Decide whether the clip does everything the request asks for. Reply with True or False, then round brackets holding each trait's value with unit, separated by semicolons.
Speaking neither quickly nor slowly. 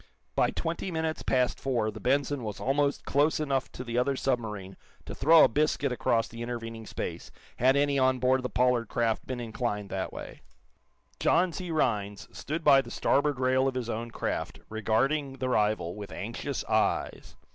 True (180 wpm)